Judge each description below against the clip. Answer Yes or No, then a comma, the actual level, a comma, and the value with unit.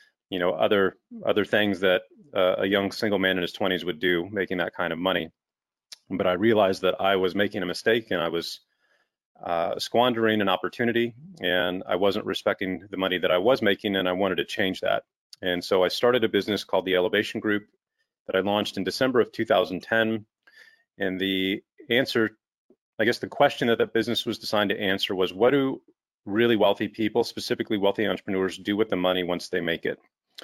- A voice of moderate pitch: No, low, 100 Hz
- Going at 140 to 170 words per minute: No, average, 200 wpm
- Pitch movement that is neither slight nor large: Yes, average, 3.4 semitones